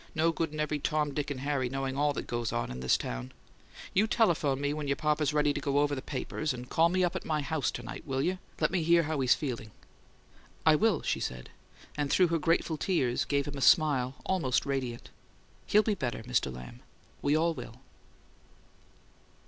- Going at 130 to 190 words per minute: No, fast, 205 wpm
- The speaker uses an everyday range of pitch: Yes, average, 3.4 semitones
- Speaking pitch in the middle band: Yes, medium, 145 Hz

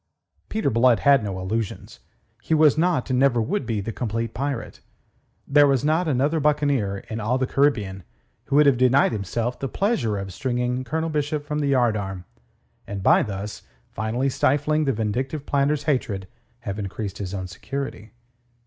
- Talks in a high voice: No, low, 125 Hz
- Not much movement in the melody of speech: No, average, 5.3 semitones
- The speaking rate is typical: Yes, average, 165 wpm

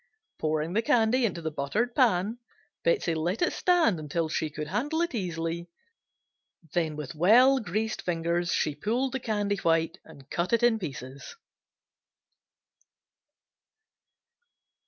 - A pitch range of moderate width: No, wide, 6.5 semitones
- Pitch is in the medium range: Yes, medium, 180 Hz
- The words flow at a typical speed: No, slow, 130 wpm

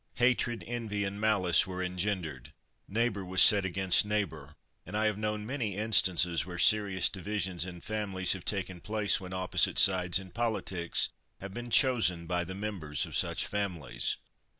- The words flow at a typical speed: Yes, average, 160 wpm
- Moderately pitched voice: No, very low, 95 Hz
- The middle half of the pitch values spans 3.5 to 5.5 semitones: No, average, 2.9 semitones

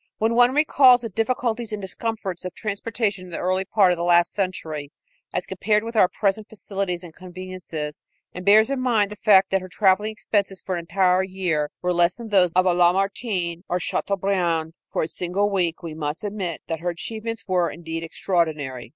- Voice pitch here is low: No, medium, 185 Hz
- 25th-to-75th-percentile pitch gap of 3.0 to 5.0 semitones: Yes, average, 3.5 semitones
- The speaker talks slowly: No, average, 195 wpm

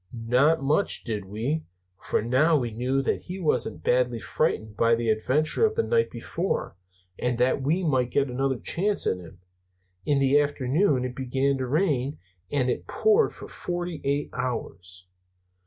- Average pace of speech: Yes, average, 165 wpm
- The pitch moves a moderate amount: Yes, average, 4.1 semitones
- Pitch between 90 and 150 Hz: Yes, low, 135 Hz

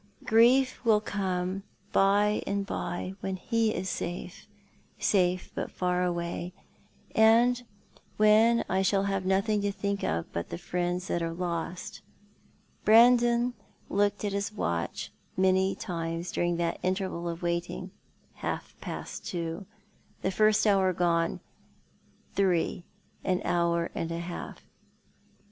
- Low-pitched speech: No, high, 190 Hz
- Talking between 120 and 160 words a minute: Yes, slow, 135 wpm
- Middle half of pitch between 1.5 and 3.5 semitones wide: Yes, average, 3.1 semitones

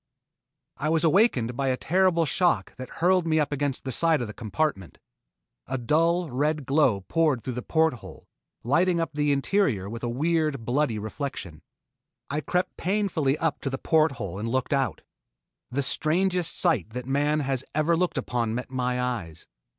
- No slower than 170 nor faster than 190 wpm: Yes, average, 175 wpm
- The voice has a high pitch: No, medium, 140 Hz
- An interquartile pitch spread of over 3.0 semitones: Yes, average, 4.7 semitones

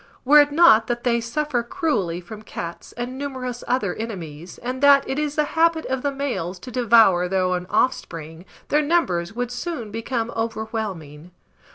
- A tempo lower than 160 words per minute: No, average, 170 wpm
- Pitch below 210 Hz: No, high, 235 Hz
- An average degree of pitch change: No, wide, 7.0 semitones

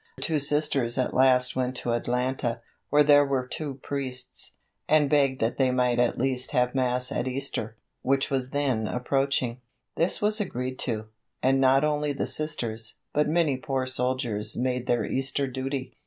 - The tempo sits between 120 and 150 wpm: No, average, 165 wpm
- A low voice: Yes, low, 130 Hz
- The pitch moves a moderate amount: No, narrow, 2.0 semitones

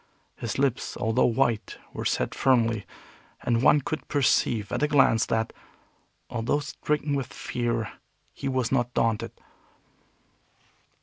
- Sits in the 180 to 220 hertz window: No, low, 120 Hz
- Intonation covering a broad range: No, average, 3.2 semitones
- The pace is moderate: No, slow, 125 wpm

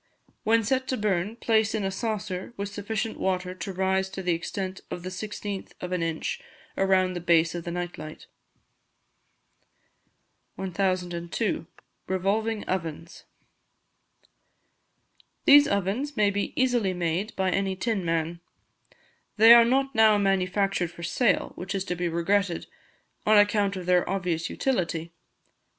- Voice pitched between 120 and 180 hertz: No, high, 190 Hz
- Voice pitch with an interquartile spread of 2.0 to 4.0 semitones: Yes, average, 3.2 semitones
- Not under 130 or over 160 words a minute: Yes, average, 140 wpm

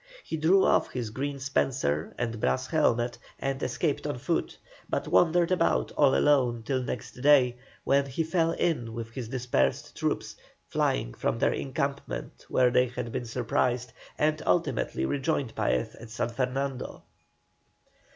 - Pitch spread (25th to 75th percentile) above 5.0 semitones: No, average, 3.3 semitones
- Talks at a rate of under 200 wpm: Yes, average, 150 wpm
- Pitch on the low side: Yes, low, 125 Hz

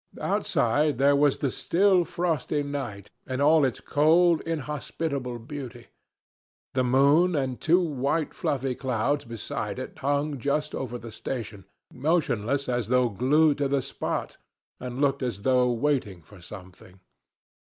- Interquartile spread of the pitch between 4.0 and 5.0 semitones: No, average, 3.4 semitones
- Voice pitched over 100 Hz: Yes, low, 135 Hz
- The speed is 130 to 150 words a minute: Yes, average, 140 wpm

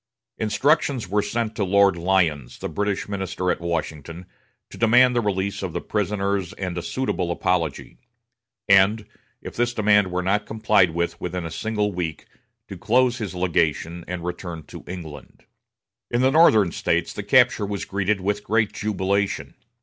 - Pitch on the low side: Yes, low, 100 Hz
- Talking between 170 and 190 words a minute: No, average, 160 wpm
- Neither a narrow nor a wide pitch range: Yes, average, 3.3 semitones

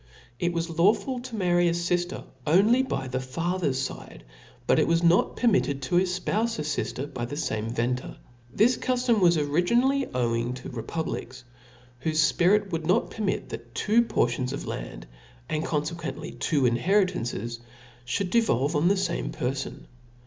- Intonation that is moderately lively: No, wide, 6.9 semitones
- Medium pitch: Yes, medium, 170 Hz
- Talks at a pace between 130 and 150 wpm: No, average, 165 wpm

